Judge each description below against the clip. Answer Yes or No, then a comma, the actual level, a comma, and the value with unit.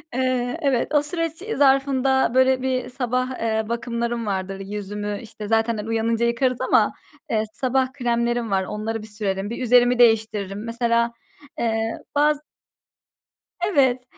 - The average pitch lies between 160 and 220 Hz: No, high, 235 Hz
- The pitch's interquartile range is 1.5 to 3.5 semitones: Yes, average, 2.8 semitones